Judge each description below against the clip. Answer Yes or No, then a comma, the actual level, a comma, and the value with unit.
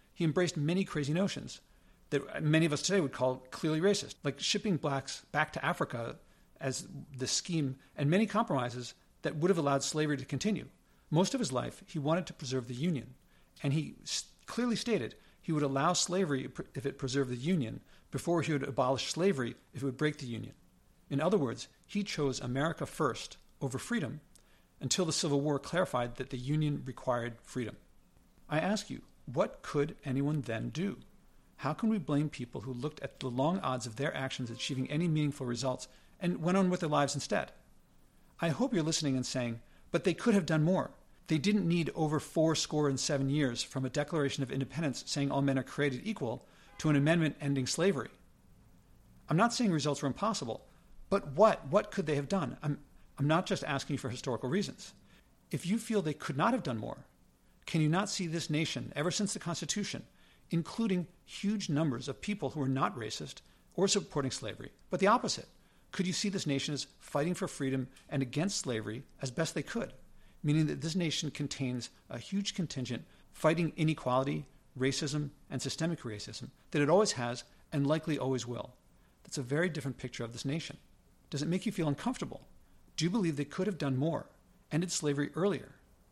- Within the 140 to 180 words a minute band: No, average, 190 wpm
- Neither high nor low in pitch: Yes, medium, 150 Hz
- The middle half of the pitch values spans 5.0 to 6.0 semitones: No, average, 4.4 semitones